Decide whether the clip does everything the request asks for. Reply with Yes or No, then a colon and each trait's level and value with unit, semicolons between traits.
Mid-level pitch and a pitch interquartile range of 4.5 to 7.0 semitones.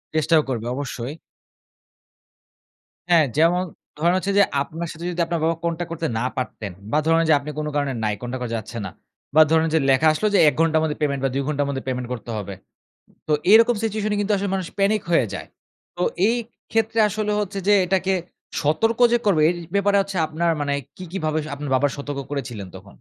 Yes: medium, 160 Hz; wide, 5.6 semitones